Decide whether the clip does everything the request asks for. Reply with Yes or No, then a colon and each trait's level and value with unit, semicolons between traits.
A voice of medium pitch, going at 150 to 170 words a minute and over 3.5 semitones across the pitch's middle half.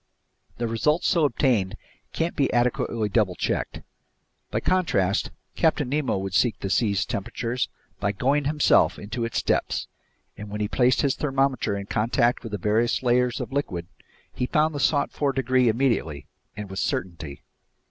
No: low, 120 Hz; average, 160 wpm; average, 5.0 semitones